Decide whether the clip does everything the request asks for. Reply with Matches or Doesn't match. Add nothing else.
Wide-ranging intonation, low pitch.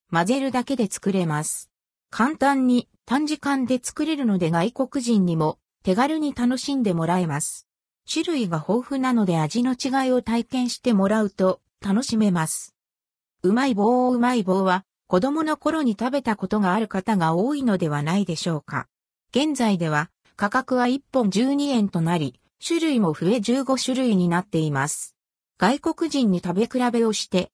Doesn't match